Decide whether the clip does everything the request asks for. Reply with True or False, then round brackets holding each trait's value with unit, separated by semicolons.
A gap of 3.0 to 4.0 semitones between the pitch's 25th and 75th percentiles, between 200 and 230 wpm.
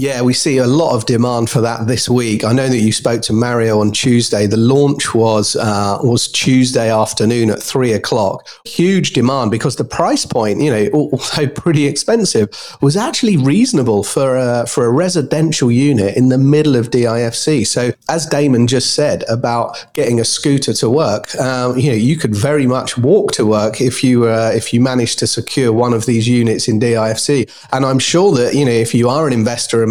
True (3.6 semitones; 205 wpm)